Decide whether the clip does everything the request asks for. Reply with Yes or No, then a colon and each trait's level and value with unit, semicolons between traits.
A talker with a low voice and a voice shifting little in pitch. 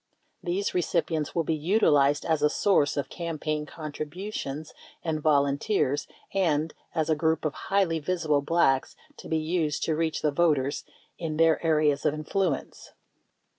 No: medium, 155 Hz; narrow, 2.3 semitones